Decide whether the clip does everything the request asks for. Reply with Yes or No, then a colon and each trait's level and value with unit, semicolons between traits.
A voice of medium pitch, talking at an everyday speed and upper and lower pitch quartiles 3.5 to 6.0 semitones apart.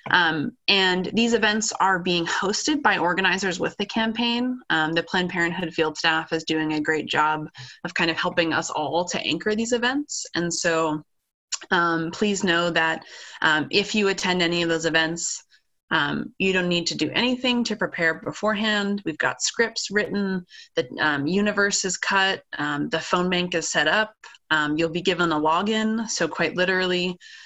Yes: medium, 180 Hz; average, 180 wpm; average, 4.3 semitones